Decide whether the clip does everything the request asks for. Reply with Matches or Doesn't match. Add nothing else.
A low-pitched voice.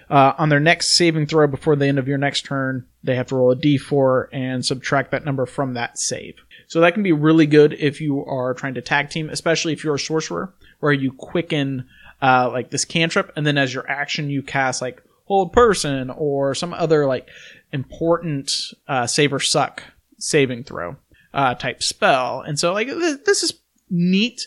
Doesn't match